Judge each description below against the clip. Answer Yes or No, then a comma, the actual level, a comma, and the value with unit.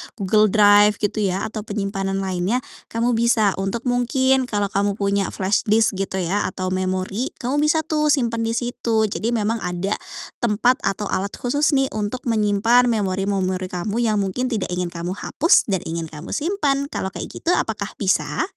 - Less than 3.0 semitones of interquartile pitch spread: No, average, 3.8 semitones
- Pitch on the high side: Yes, high, 210 Hz